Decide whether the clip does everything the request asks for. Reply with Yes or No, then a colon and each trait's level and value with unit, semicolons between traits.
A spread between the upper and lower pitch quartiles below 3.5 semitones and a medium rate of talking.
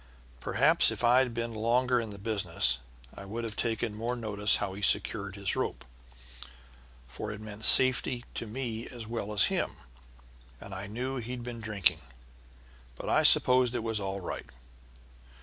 Yes: average, 3.0 semitones; average, 165 wpm